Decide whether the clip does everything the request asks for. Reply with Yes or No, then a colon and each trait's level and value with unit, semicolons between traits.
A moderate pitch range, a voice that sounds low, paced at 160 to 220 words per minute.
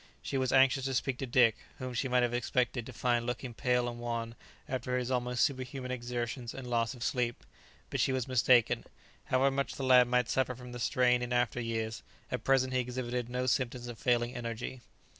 No: narrow, 1.2 semitones; low, 125 Hz; fast, 205 wpm